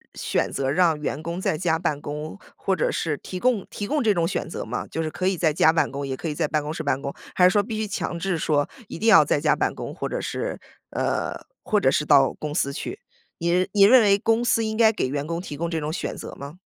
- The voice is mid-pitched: Yes, medium, 165 Hz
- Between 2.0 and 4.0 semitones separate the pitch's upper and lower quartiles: No, average, 4.8 semitones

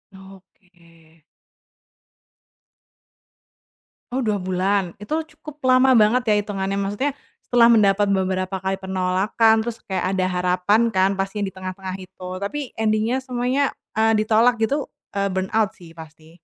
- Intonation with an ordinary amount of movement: Yes, average, 3.2 semitones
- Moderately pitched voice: No, high, 200 Hz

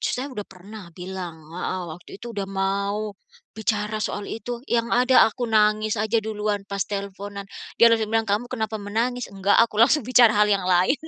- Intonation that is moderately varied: No, narrow, 2.3 semitones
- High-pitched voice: Yes, high, 210 Hz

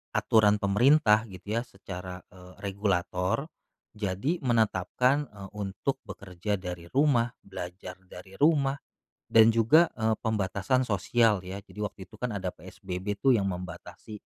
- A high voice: No, low, 105 Hz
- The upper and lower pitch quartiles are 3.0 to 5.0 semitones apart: Yes, average, 3.9 semitones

